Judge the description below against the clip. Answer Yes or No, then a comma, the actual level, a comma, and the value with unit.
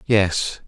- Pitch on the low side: Yes, low, 100 Hz